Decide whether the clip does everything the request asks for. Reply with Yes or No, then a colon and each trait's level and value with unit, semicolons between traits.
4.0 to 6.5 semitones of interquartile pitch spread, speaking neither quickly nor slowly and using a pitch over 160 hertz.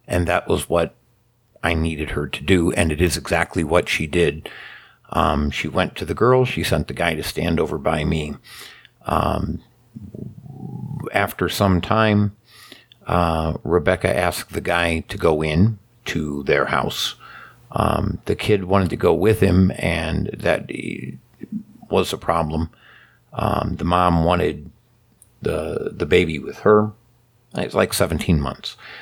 No: average, 4.5 semitones; average, 150 wpm; very low, 90 Hz